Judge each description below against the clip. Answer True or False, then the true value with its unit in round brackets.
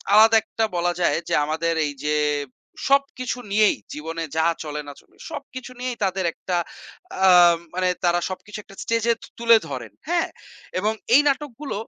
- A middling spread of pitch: False (6.6 semitones)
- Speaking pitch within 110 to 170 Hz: False (200 Hz)